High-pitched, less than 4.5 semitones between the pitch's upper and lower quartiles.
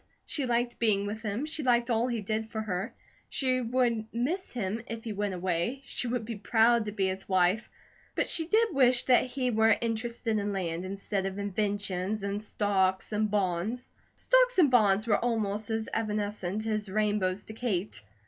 Yes: high, 215 Hz; average, 3.1 semitones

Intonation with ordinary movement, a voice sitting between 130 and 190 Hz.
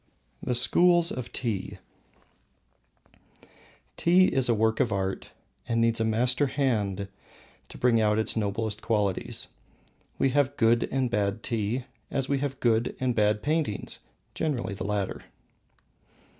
No: average, 3.9 semitones; low, 115 Hz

